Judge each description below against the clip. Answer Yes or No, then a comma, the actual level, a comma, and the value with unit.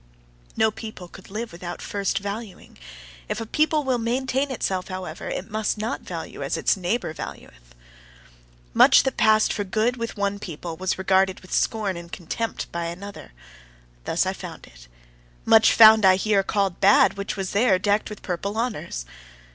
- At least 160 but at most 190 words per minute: Yes, average, 170 wpm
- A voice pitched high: Yes, high, 200 Hz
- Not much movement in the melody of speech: No, average, 3.1 semitones